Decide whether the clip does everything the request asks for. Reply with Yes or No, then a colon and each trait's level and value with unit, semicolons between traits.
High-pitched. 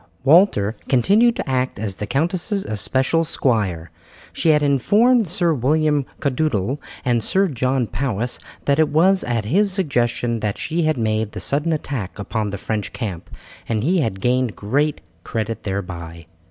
No: low, 130 Hz